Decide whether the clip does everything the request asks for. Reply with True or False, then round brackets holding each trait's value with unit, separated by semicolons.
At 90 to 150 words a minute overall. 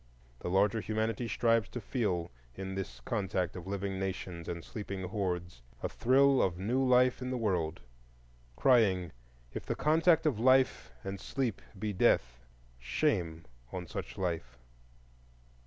True (140 wpm)